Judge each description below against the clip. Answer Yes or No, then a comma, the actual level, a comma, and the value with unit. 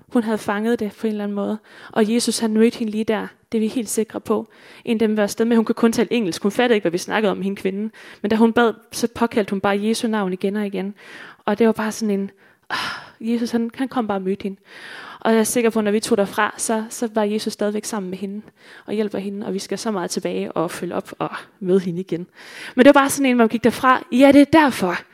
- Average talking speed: No, fast, 280 wpm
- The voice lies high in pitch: Yes, high, 220 Hz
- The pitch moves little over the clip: Yes, narrow, 2.3 semitones